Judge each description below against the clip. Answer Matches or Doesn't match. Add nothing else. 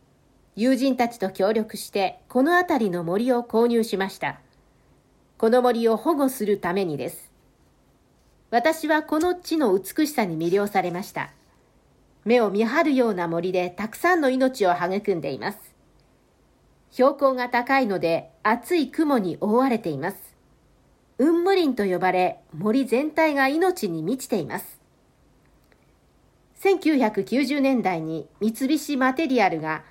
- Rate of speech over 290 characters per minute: Doesn't match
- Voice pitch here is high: Matches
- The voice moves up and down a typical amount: Doesn't match